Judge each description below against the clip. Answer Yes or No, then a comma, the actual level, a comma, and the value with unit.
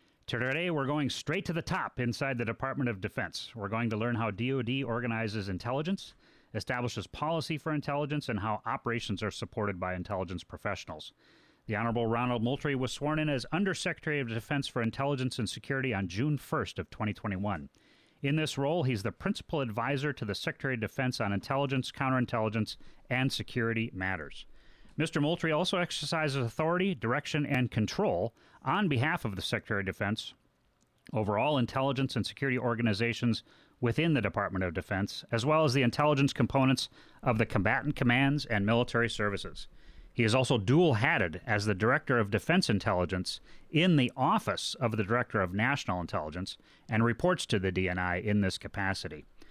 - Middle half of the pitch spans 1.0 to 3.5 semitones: No, average, 4.8 semitones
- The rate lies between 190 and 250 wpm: No, average, 165 wpm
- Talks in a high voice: No, low, 120 Hz